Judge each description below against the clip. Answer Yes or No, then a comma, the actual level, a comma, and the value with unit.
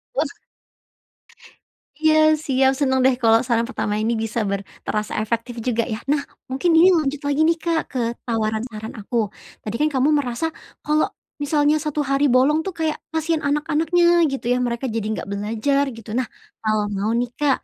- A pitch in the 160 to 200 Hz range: No, very high, 260 Hz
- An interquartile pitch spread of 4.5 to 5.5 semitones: Yes, average, 4.9 semitones